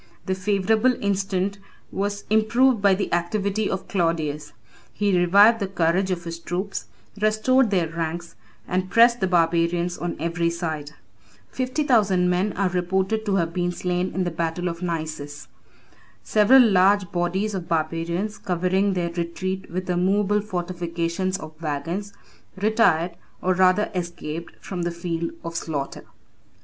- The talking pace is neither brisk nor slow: Yes, average, 145 wpm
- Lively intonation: No, average, 3.0 semitones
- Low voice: No, medium, 180 Hz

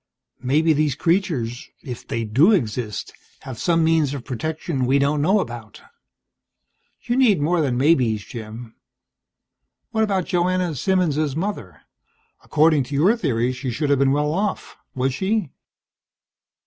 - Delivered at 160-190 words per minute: No, average, 140 wpm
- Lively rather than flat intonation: Yes, wide, 5.7 semitones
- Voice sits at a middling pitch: Yes, medium, 145 Hz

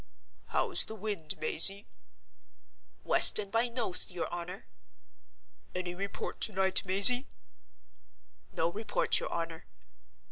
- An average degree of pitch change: Yes, average, 3.7 semitones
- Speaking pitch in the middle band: No, high, 195 Hz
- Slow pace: Yes, slow, 110 wpm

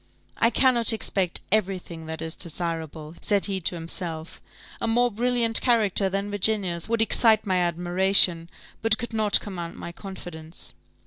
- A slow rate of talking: No, average, 150 wpm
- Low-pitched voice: No, high, 190 Hz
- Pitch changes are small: No, average, 4.5 semitones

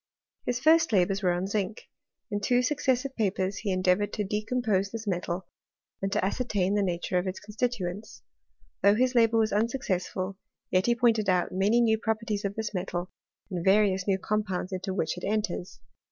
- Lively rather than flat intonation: No, average, 3.2 semitones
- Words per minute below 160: No, average, 180 wpm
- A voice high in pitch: Yes, high, 205 Hz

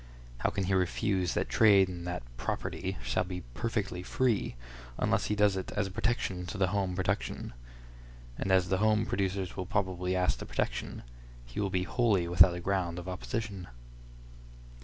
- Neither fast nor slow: Yes, average, 175 wpm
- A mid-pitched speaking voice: No, very low, 95 Hz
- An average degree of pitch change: No, narrow, 2.3 semitones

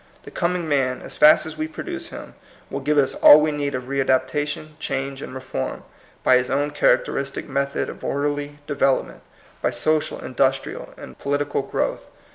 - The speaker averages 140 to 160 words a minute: No, average, 175 wpm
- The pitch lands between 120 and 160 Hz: Yes, medium, 140 Hz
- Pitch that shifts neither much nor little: No, narrow, 2.0 semitones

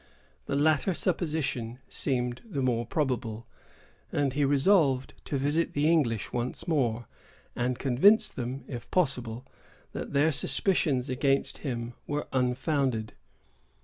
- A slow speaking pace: Yes, slow, 120 wpm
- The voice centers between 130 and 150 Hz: Yes, low, 135 Hz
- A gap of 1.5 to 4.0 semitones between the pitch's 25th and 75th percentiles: Yes, average, 3.2 semitones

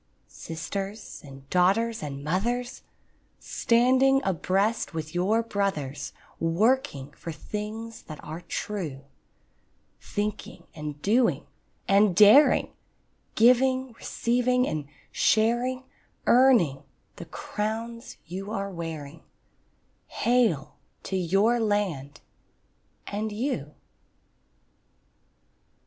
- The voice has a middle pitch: No, high, 205 Hz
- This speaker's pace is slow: Yes, slow, 85 wpm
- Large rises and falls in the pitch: Yes, wide, 6.1 semitones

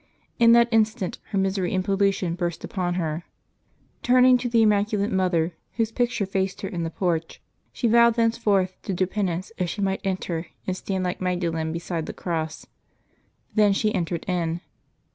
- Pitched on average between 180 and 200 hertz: Yes, high, 190 Hz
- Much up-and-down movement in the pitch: No, average, 3.5 semitones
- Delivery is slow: No, average, 170 wpm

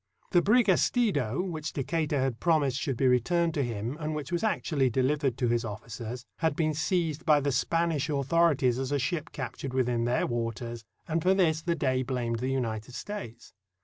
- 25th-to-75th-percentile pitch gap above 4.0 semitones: Yes, average, 4.9 semitones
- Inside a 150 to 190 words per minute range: Yes, average, 185 wpm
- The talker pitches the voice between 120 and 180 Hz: Yes, medium, 140 Hz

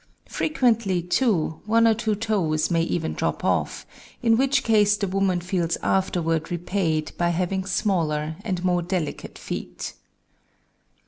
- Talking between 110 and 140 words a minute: Yes, slow, 135 wpm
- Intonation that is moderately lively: Yes, average, 4.1 semitones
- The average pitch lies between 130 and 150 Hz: No, medium, 185 Hz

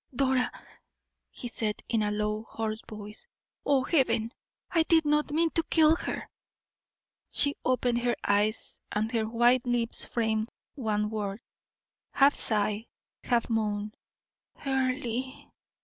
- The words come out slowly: Yes, slow, 125 wpm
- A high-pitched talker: Yes, high, 235 Hz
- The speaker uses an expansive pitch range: No, average, 3.6 semitones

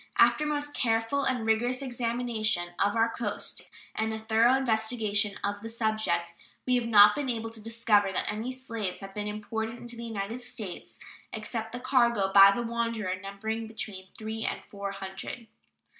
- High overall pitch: Yes, high, 220 Hz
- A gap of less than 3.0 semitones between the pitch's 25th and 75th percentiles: Yes, narrow, 2.4 semitones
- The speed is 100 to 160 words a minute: No, average, 175 wpm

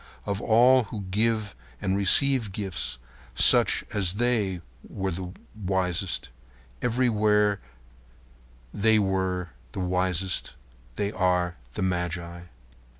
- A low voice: Yes, very low, 95 Hz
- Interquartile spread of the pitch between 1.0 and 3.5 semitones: Yes, average, 3.0 semitones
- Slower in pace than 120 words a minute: Yes, slow, 90 wpm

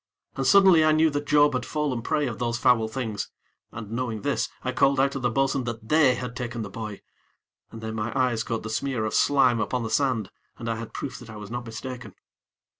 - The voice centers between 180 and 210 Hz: No, low, 125 Hz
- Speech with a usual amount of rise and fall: Yes, average, 3.3 semitones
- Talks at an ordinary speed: No, fast, 230 wpm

